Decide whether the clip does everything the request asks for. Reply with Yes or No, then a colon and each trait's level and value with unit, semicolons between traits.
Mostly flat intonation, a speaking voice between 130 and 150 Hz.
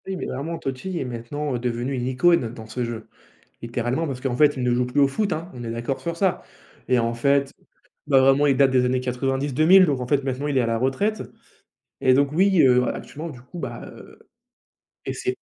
No: average, 3.3 semitones; low, 135 Hz